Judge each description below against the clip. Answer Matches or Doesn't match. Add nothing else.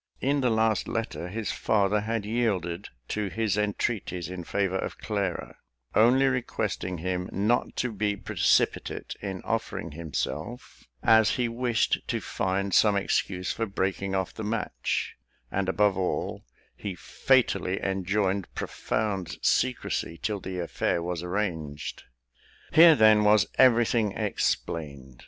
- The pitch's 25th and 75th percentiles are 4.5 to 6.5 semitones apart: Doesn't match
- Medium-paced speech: Doesn't match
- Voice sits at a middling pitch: Doesn't match